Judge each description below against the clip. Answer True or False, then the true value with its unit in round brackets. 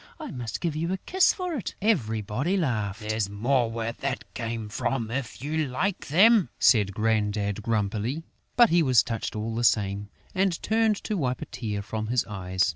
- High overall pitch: False (115 Hz)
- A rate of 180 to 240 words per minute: True (185 wpm)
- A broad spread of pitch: True (7.4 semitones)